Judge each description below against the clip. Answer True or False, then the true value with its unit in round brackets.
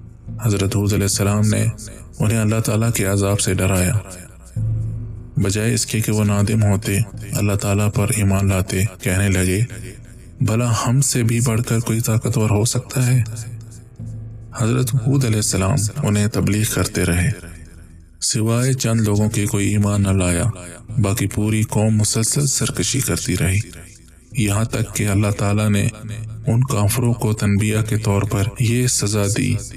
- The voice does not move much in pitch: True (2.3 semitones)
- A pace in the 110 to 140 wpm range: False (155 wpm)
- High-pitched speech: False (110 Hz)